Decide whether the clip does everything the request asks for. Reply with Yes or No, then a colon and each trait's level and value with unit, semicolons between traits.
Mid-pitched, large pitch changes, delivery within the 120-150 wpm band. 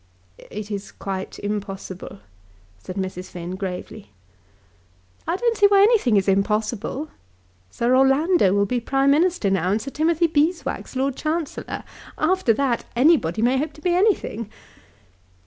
No: very high, 250 Hz; wide, 8.1 semitones; average, 140 wpm